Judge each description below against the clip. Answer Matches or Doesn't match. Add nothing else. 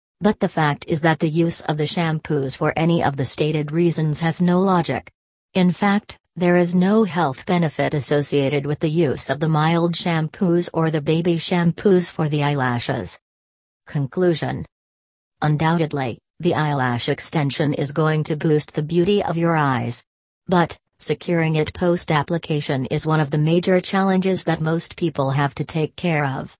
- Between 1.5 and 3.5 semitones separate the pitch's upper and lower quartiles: Matches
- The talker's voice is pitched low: Doesn't match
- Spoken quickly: Doesn't match